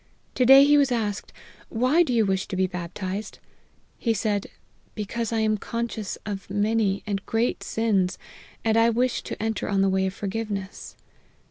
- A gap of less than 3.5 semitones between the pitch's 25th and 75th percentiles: Yes, average, 3.0 semitones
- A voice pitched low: No, high, 215 Hz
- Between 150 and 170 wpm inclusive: No, average, 185 wpm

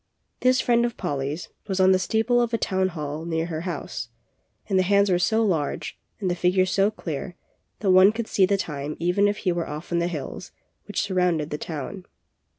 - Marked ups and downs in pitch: No, average, 3.7 semitones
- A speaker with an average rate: No, fast, 210 wpm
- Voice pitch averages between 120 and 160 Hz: No, medium, 185 Hz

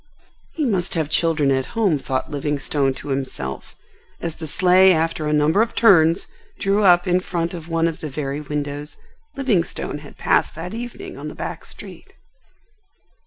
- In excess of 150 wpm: Yes, average, 165 wpm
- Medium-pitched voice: Yes, medium, 165 Hz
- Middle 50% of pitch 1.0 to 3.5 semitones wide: No, average, 4.0 semitones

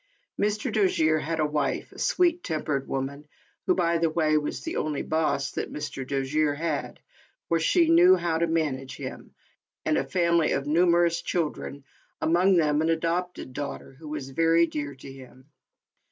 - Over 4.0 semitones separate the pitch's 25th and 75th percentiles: No, average, 2.8 semitones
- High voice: No, medium, 160 Hz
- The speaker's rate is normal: Yes, average, 170 wpm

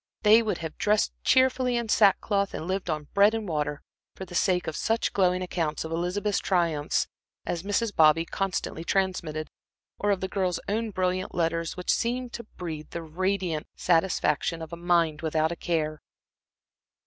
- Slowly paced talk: No, average, 170 wpm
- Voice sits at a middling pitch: Yes, medium, 180 Hz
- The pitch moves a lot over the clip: No, average, 3.7 semitones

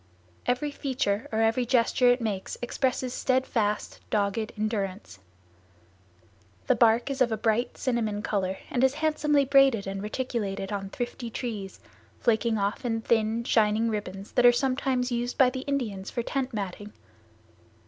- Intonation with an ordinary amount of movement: Yes, average, 3.4 semitones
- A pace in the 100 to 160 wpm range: Yes, average, 150 wpm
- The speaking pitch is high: Yes, high, 230 Hz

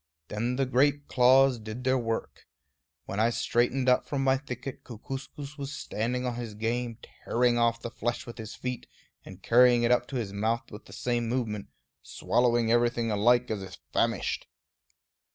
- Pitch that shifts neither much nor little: No, narrow, 1.9 semitones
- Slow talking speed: No, average, 170 wpm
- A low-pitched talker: Yes, low, 120 Hz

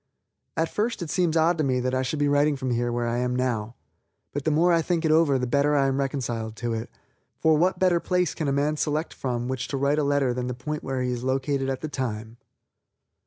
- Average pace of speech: No, fast, 250 wpm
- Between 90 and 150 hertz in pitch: Yes, medium, 140 Hz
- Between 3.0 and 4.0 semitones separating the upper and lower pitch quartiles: Yes, average, 3.6 semitones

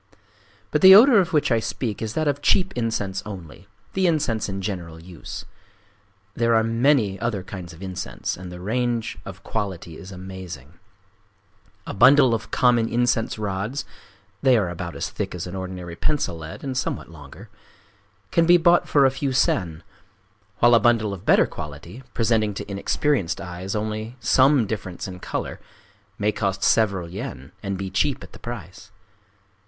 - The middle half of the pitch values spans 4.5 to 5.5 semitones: Yes, average, 4.8 semitones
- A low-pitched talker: Yes, low, 105 Hz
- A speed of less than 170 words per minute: Yes, average, 160 wpm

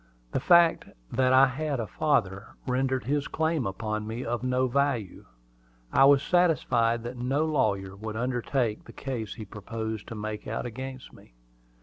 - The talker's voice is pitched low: Yes, low, 125 Hz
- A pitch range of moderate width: Yes, average, 3.7 semitones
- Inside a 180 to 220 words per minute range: No, average, 160 wpm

